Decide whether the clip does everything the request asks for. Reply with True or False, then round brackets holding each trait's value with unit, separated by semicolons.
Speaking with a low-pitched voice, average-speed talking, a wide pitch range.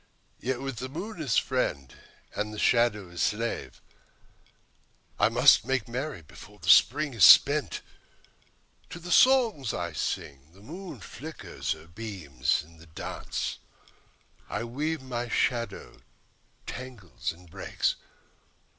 False (115 Hz; 130 wpm; 7.9 semitones)